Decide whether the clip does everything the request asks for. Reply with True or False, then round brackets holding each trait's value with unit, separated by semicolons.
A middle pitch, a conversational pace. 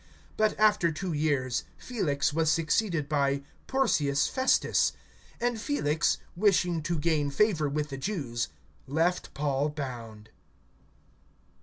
False (155 Hz; 115 wpm)